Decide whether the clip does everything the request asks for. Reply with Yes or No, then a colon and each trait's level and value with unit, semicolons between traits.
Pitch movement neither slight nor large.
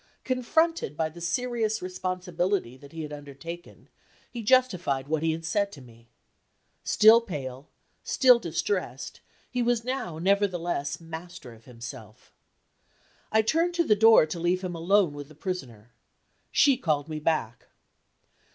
No: wide, 6.8 semitones